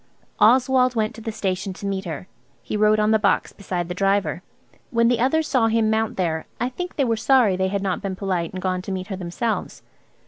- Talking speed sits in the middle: No, fast, 230 wpm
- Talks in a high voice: Yes, high, 205 Hz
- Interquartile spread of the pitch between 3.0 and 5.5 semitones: Yes, average, 3.6 semitones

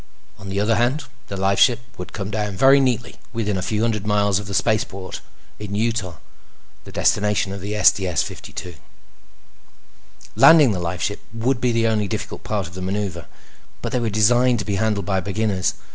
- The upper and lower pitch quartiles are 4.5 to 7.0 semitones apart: No, average, 2.8 semitones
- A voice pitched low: Yes, low, 105 Hz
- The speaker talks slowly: No, average, 180 wpm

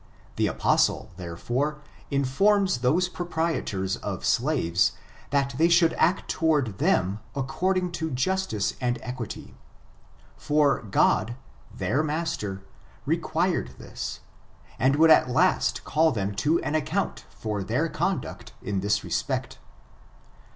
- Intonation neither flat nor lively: No, wide, 6.9 semitones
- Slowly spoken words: Yes, slow, 115 wpm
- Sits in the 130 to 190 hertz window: Yes, medium, 140 Hz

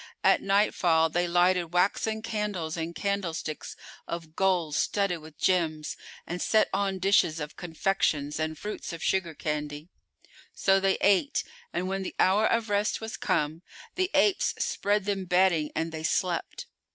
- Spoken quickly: No, average, 150 wpm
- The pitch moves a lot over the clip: No, average, 3.6 semitones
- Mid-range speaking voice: Yes, medium, 180 Hz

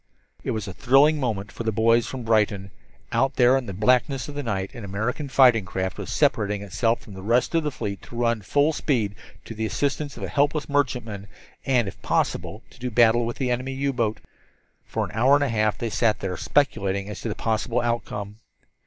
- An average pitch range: Yes, average, 4.0 semitones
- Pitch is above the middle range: No, low, 115 Hz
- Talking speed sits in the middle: No, fast, 215 wpm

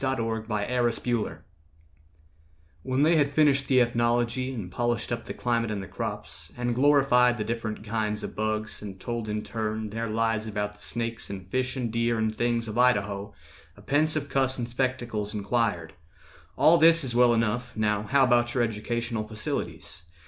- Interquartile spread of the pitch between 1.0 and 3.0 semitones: Yes, narrow, 2.5 semitones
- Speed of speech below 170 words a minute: No, average, 175 wpm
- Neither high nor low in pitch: No, low, 115 Hz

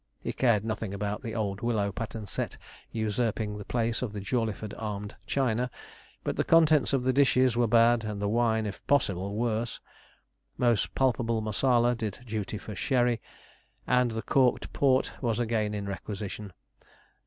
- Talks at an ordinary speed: Yes, average, 160 wpm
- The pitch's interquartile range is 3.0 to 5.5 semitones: No, narrow, 2.6 semitones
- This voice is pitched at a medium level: No, low, 115 Hz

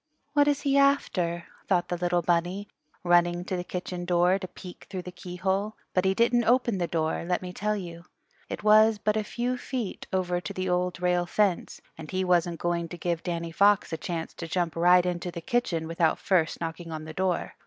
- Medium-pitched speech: Yes, medium, 180 Hz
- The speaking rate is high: Yes, fast, 210 wpm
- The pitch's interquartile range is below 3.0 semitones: Yes, narrow, 2.5 semitones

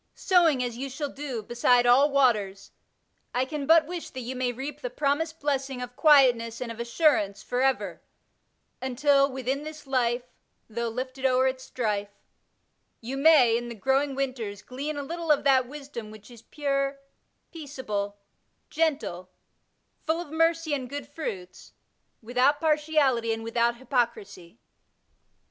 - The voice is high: Yes, very high, 260 Hz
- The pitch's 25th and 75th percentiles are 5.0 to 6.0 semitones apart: No, average, 3.6 semitones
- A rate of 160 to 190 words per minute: No, average, 150 wpm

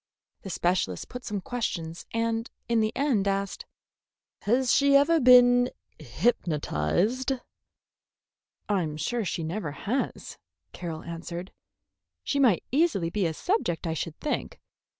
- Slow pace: Yes, slow, 125 wpm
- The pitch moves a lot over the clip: Yes, wide, 6.7 semitones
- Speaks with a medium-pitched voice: No, high, 205 Hz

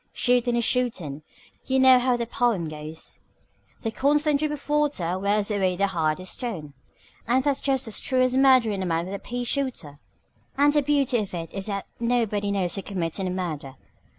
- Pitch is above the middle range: Yes, high, 220 Hz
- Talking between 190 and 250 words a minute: Yes, average, 195 wpm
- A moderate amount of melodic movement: No, wide, 6.0 semitones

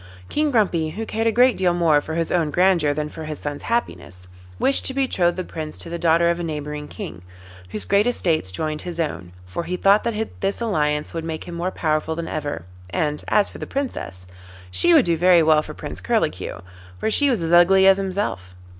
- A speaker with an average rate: No, fast, 215 wpm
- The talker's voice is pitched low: No, medium, 170 Hz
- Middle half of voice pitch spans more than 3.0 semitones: Yes, average, 4.1 semitones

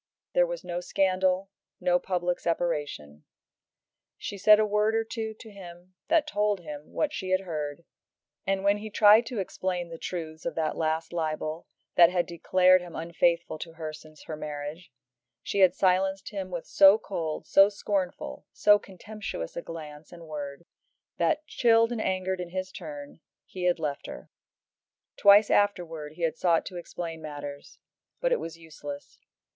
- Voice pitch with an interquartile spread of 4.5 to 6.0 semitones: No, average, 3.8 semitones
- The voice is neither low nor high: Yes, medium, 180 Hz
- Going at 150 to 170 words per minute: Yes, average, 165 wpm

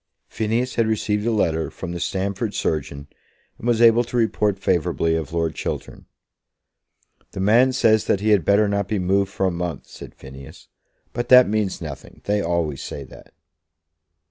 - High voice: No, low, 100 Hz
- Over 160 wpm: Yes, average, 170 wpm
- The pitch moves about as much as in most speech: Yes, average, 4.7 semitones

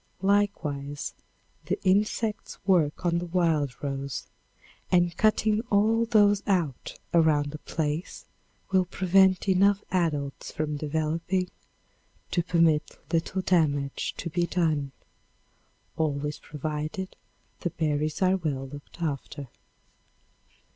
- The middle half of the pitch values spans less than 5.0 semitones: Yes, average, 4.1 semitones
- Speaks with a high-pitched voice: No, medium, 165 Hz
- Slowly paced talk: Yes, slow, 105 wpm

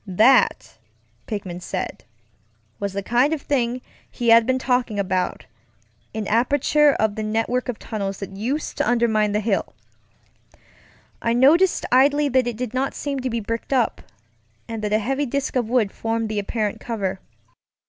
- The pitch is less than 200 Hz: No, high, 235 Hz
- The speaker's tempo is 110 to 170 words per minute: Yes, average, 160 wpm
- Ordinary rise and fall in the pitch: Yes, average, 3.4 semitones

